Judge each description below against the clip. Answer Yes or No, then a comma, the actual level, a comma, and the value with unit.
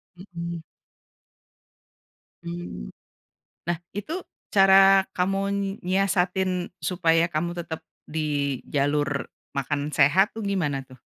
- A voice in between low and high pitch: Yes, medium, 170 Hz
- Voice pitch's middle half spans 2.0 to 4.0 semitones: No, average, 4.5 semitones